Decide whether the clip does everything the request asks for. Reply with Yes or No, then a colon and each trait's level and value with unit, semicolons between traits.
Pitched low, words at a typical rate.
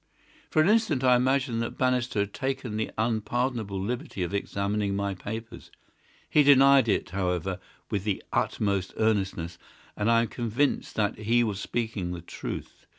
Yes: low, 110 Hz; average, 155 wpm